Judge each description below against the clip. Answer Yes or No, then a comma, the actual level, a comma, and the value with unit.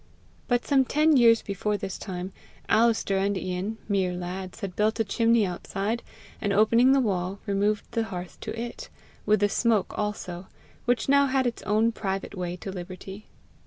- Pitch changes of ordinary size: Yes, average, 3.4 semitones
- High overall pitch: Yes, high, 205 Hz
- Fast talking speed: No, average, 170 wpm